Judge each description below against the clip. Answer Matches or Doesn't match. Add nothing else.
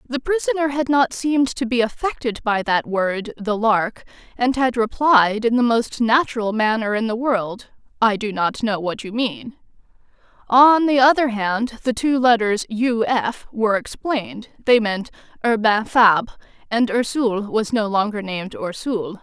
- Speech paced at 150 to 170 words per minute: Matches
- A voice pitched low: Doesn't match